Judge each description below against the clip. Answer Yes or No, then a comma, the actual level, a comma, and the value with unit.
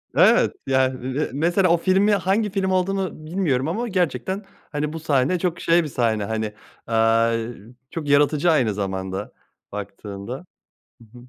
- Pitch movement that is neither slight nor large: No, wide, 8.1 semitones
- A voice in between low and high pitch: Yes, medium, 150 Hz